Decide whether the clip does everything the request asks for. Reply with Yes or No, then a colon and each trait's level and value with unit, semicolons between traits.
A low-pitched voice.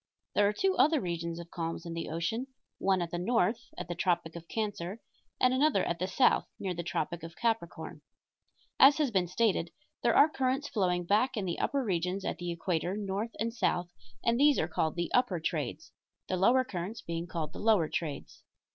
No: medium, 185 Hz